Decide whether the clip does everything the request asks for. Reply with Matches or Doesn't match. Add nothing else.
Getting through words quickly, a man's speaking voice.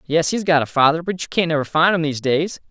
Matches